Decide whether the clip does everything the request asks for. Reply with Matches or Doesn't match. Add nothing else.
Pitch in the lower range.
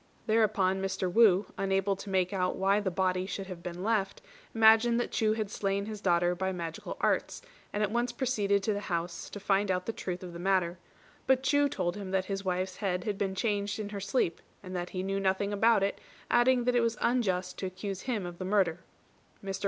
Doesn't match